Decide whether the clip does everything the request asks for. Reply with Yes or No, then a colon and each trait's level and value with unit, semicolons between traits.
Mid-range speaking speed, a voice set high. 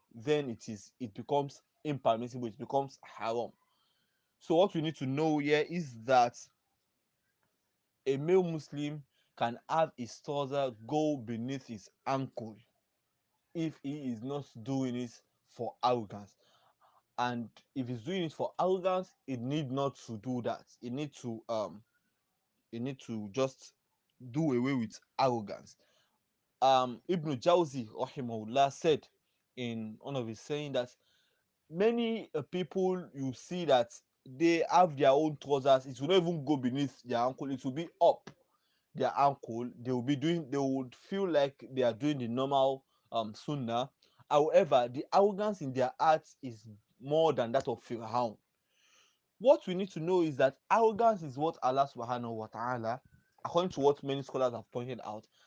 No: average, 160 wpm; low, 135 Hz